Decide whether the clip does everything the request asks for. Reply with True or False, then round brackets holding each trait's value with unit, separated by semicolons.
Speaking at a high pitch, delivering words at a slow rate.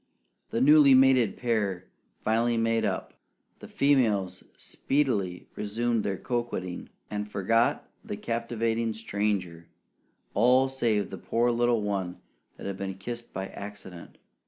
False (115 Hz; 125 wpm)